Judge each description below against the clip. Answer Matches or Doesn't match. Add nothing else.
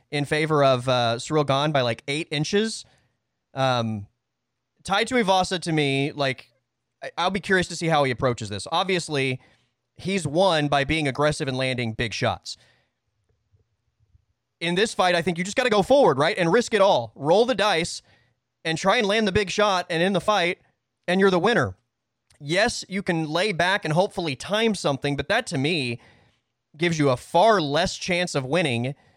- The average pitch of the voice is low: Doesn't match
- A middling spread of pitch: Doesn't match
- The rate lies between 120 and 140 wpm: Doesn't match